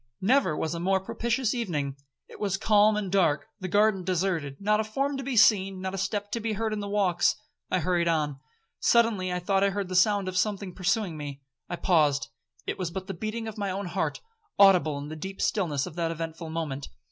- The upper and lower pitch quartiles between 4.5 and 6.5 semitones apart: No, average, 3.9 semitones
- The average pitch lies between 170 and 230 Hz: Yes, high, 190 Hz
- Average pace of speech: No, fast, 210 wpm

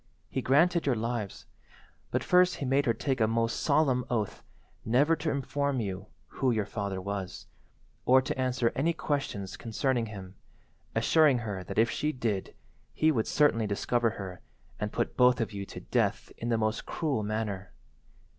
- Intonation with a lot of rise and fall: No, average, 4.6 semitones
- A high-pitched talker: No, low, 120 Hz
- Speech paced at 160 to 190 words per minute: Yes, average, 170 wpm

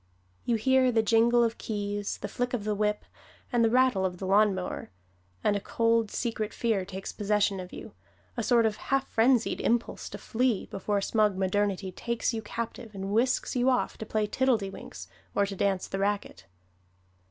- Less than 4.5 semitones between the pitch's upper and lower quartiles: Yes, average, 2.9 semitones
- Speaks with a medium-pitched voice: No, high, 215 Hz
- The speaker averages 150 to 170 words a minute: No, average, 180 wpm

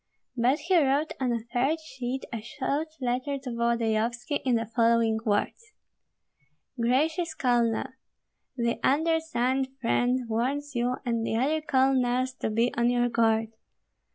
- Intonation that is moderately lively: Yes, average, 3.0 semitones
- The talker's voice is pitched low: No, high, 245 Hz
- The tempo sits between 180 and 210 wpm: No, slow, 135 wpm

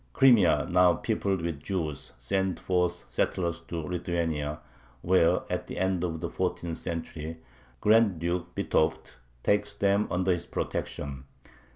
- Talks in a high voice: No, very low, 85 Hz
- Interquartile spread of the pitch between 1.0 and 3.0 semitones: Yes, narrow, 2.5 semitones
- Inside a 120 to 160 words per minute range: Yes, slow, 135 wpm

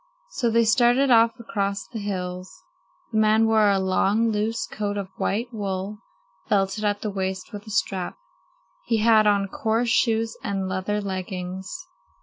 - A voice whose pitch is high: Yes, high, 210 Hz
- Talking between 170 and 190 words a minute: No, average, 155 wpm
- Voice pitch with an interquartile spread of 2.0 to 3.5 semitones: Yes, narrow, 2.6 semitones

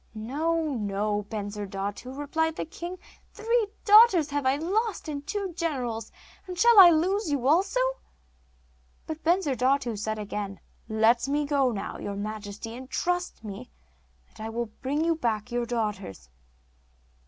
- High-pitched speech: Yes, very high, 270 Hz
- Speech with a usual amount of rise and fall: No, wide, 7.5 semitones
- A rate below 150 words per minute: Yes, average, 140 wpm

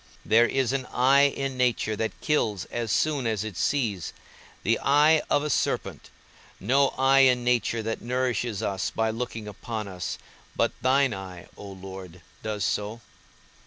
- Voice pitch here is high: No, low, 115 Hz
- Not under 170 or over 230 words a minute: No, average, 160 wpm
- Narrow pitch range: No, average, 4.3 semitones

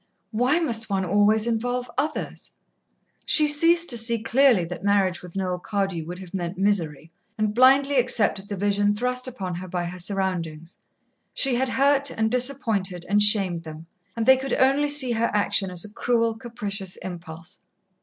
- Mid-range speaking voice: No, high, 210 Hz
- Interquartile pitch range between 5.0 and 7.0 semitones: Yes, average, 5.3 semitones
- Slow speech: No, average, 170 wpm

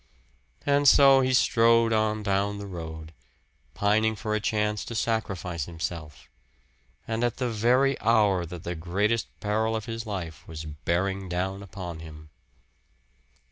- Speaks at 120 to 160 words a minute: Yes, average, 140 wpm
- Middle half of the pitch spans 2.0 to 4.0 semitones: No, average, 4.5 semitones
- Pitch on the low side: Yes, low, 105 Hz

